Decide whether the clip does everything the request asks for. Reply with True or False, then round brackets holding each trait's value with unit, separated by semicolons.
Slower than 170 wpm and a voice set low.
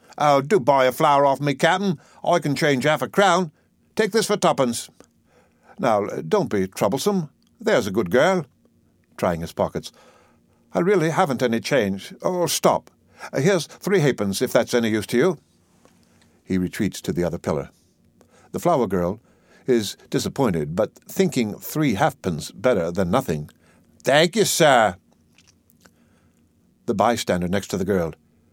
True (150 wpm; 120 Hz)